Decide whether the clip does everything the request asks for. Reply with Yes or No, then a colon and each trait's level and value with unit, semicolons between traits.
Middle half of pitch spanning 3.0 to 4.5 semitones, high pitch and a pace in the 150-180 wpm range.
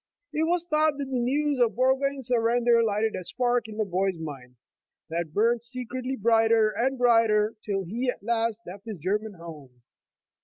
Yes: average, 3.8 semitones; high, 230 Hz; average, 175 wpm